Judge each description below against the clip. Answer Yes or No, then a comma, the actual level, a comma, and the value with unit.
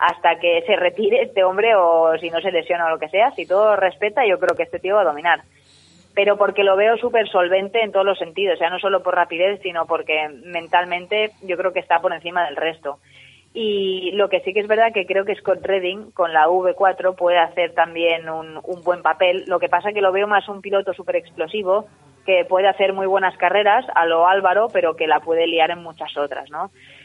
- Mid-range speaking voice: Yes, medium, 180 Hz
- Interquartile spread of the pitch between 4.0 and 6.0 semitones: No, average, 2.7 semitones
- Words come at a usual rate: No, fast, 235 wpm